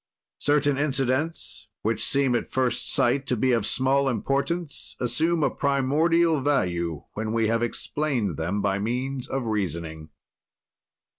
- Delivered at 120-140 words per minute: Yes, slow, 135 wpm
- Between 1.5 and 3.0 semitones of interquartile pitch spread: No, average, 4.8 semitones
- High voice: No, low, 130 Hz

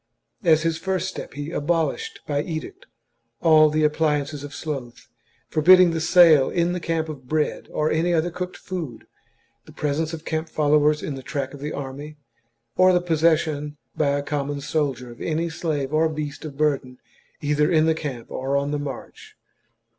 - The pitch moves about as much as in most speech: No, narrow, 2.3 semitones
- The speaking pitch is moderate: Yes, medium, 155 Hz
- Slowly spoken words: No, average, 175 wpm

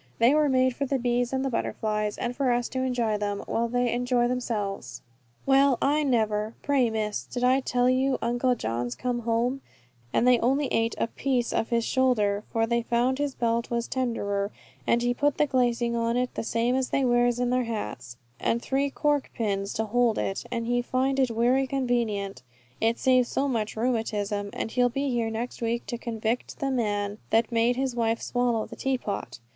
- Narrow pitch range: Yes, narrow, 2.2 semitones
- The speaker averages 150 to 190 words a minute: No, average, 200 wpm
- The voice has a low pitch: No, high, 240 Hz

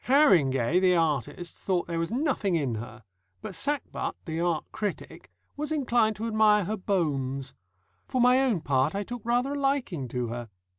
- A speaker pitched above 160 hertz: Yes, medium, 185 Hz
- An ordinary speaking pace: Yes, average, 170 wpm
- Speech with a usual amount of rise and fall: No, wide, 9.0 semitones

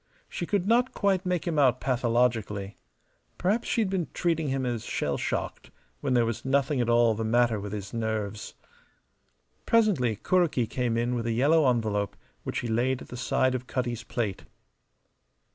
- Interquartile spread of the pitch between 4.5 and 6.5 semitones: Yes, average, 5.3 semitones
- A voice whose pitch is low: Yes, low, 125 Hz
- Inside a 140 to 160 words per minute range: No, average, 175 wpm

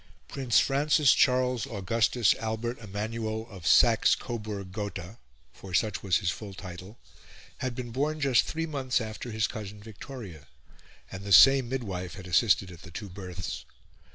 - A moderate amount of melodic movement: Yes, average, 4.5 semitones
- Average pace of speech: Yes, average, 155 wpm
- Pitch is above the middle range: No, low, 110 Hz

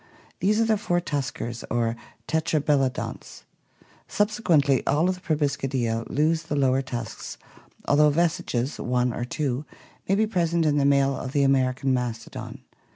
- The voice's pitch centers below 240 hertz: Yes, medium, 140 Hz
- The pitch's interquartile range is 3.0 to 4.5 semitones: Yes, average, 4.2 semitones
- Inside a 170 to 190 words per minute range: No, average, 145 wpm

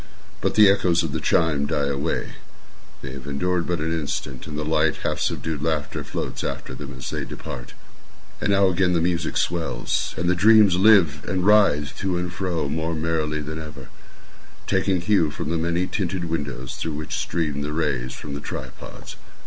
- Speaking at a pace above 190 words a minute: No, average, 180 wpm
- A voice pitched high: No, very low, 80 Hz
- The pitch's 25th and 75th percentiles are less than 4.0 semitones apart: Yes, average, 3.4 semitones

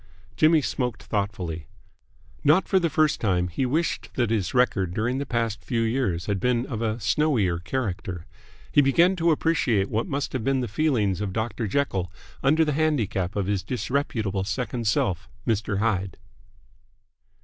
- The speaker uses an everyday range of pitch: No, wide, 5.7 semitones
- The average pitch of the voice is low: Yes, low, 115 Hz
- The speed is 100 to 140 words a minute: No, average, 160 wpm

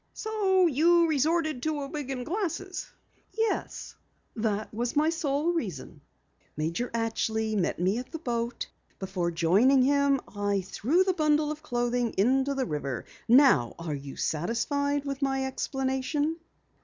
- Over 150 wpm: No, average, 145 wpm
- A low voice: No, very high, 265 Hz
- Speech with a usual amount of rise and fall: No, wide, 5.9 semitones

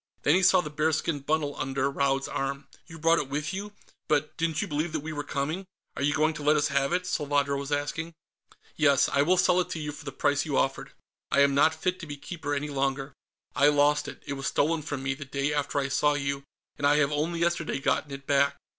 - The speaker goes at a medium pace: No, fast, 245 wpm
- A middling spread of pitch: No, narrow, 2.1 semitones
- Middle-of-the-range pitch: Yes, medium, 145 Hz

